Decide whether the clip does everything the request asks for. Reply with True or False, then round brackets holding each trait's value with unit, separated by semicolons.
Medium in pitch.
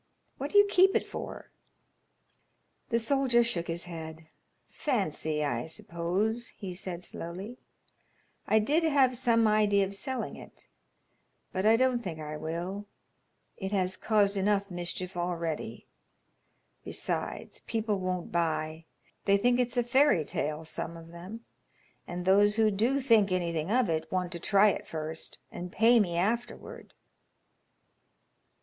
False (195 Hz)